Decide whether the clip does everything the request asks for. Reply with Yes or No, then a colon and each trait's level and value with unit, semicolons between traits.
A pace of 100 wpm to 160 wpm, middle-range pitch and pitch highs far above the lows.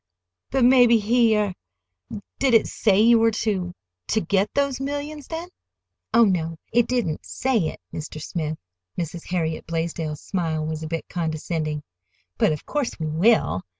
Yes: average, 145 wpm; medium, 180 Hz; wide, 6.8 semitones